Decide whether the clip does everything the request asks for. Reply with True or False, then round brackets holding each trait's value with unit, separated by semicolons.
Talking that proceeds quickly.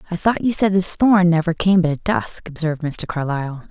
True (225 wpm)